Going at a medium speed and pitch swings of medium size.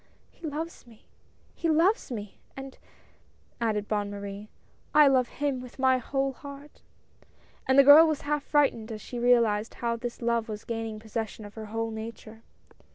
Yes: average, 170 wpm; average, 4.1 semitones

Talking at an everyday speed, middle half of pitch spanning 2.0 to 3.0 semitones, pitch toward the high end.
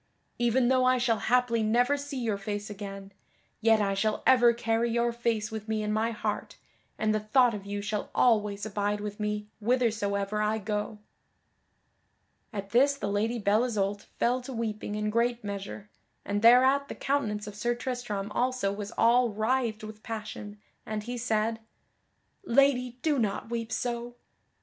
Yes: average, 165 wpm; narrow, 2.5 semitones; high, 220 Hz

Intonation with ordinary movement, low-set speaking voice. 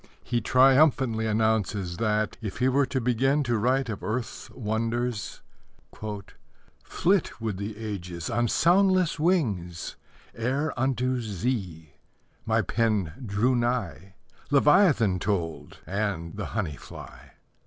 Yes: average, 4.4 semitones; low, 115 Hz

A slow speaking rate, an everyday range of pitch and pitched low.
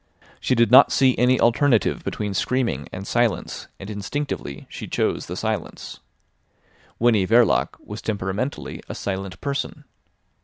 Yes: slow, 130 wpm; average, 4.5 semitones; low, 115 Hz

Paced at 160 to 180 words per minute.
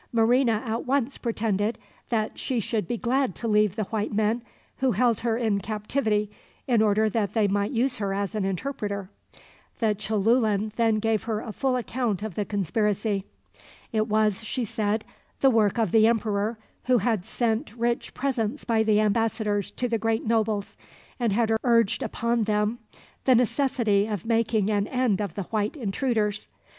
Yes: average, 170 wpm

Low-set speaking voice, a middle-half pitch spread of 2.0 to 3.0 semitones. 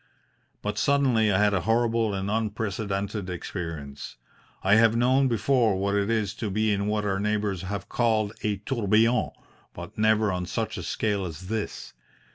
Yes: low, 105 Hz; narrow, 2.4 semitones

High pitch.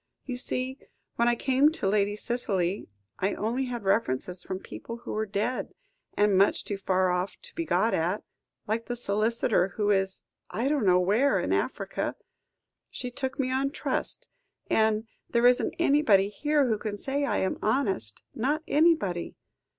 Yes: high, 220 Hz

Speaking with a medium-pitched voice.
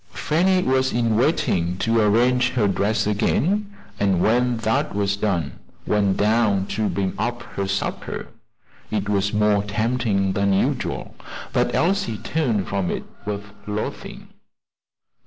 No: low, 105 Hz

